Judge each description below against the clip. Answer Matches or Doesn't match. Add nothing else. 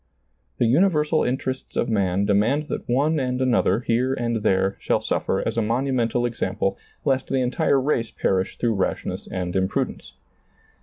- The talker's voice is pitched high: Doesn't match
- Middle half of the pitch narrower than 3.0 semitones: Doesn't match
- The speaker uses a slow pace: Doesn't match